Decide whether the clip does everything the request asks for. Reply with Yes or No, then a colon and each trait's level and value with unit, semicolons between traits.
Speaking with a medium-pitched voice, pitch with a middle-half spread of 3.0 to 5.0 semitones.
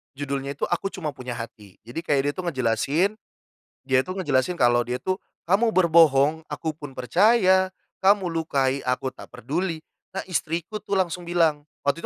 No: medium, 160 Hz; wide, 5.5 semitones